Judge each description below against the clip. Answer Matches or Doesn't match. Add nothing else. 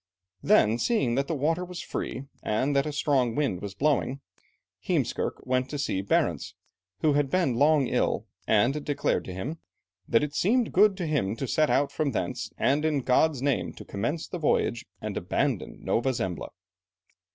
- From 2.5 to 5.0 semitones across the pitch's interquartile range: Matches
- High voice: Doesn't match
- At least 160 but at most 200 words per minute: Matches